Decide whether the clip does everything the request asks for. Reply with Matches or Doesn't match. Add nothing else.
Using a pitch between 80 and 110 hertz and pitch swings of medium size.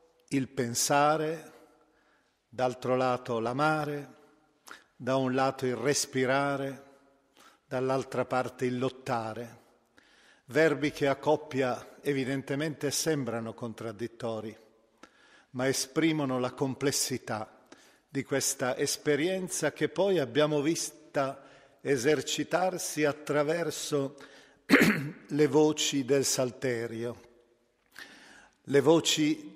Doesn't match